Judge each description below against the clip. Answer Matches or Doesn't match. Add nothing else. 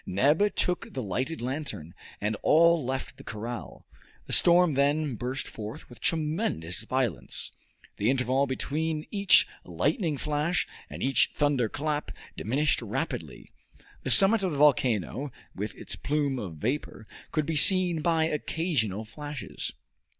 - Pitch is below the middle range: Doesn't match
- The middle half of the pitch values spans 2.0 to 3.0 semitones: Doesn't match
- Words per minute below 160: Matches